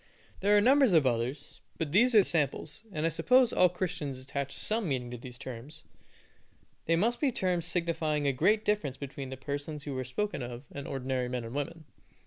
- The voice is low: No, medium, 150 Hz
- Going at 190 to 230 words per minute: Yes, average, 195 wpm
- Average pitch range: No, wide, 5.9 semitones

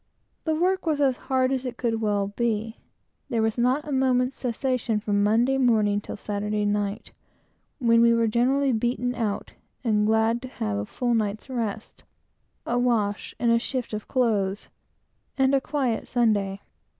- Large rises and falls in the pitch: No, average, 3.4 semitones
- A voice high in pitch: Yes, high, 235 Hz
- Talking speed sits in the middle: Yes, average, 160 wpm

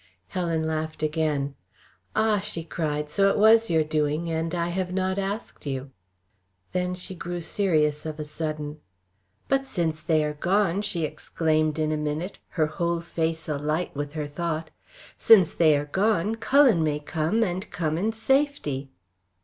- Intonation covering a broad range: No, average, 3.6 semitones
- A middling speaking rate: Yes, average, 160 wpm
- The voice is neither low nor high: Yes, medium, 165 Hz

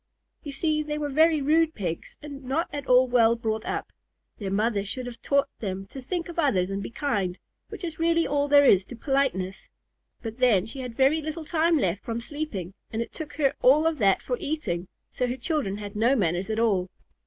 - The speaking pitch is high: Yes, very high, 255 Hz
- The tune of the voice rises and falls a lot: Yes, wide, 6.5 semitones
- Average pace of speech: No, fast, 215 wpm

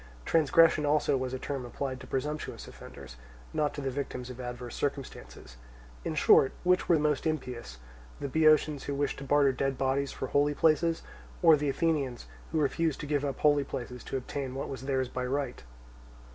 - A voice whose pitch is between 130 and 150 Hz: Yes, medium, 140 Hz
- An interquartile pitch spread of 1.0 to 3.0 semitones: Yes, narrow, 2.6 semitones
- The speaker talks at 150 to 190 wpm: Yes, average, 180 wpm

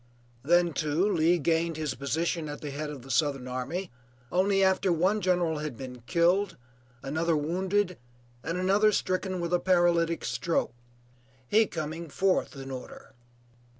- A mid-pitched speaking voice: Yes, medium, 170 Hz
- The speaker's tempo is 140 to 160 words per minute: Yes, average, 150 wpm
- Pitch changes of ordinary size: Yes, average, 3.6 semitones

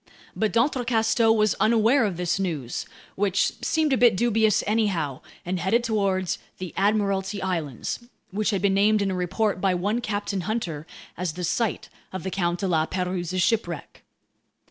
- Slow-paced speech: No, average, 155 wpm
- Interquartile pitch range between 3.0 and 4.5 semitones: Yes, average, 3.4 semitones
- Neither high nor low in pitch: No, high, 195 Hz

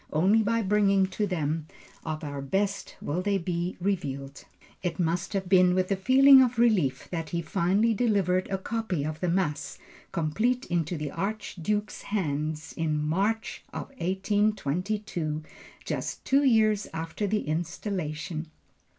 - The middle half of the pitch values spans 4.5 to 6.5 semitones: Yes, average, 4.8 semitones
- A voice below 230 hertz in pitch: Yes, medium, 185 Hz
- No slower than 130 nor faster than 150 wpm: Yes, average, 140 wpm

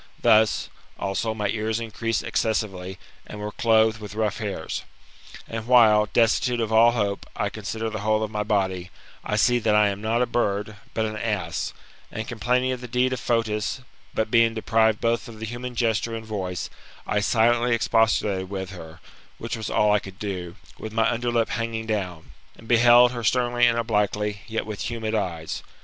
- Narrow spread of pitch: Yes, narrow, 1.9 semitones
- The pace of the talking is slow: No, average, 185 wpm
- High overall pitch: No, low, 110 Hz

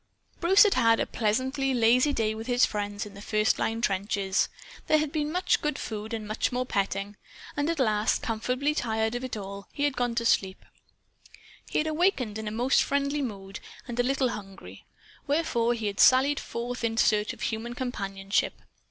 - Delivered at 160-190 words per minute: Yes, average, 185 wpm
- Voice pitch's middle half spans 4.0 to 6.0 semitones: Yes, average, 4.3 semitones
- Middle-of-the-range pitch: No, high, 235 Hz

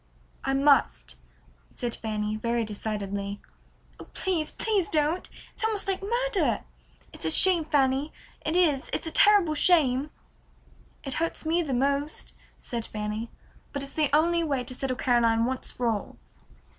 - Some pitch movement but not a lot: No, wide, 6.1 semitones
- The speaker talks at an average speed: Yes, average, 145 wpm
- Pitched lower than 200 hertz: No, very high, 275 Hz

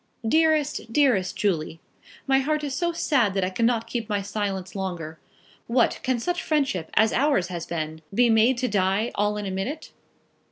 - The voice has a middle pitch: No, high, 220 Hz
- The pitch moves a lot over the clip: Yes, wide, 6.0 semitones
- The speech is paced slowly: No, average, 175 wpm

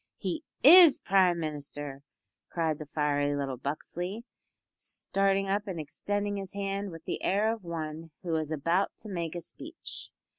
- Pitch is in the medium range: Yes, medium, 175 Hz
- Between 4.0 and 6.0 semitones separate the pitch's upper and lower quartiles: Yes, average, 4.5 semitones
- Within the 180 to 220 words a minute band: No, average, 155 wpm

